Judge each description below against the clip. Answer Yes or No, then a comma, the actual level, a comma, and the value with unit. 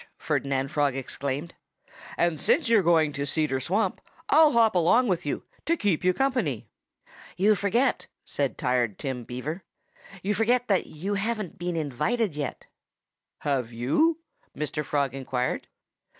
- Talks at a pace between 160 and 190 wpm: No, average, 145 wpm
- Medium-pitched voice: Yes, medium, 160 Hz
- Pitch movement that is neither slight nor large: No, wide, 7.6 semitones